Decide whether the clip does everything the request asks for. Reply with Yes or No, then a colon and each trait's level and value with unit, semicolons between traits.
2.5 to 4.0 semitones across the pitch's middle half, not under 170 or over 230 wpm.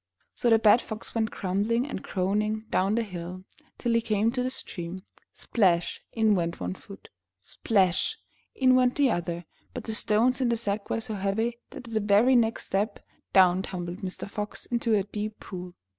Yes: average, 3.7 semitones; average, 190 wpm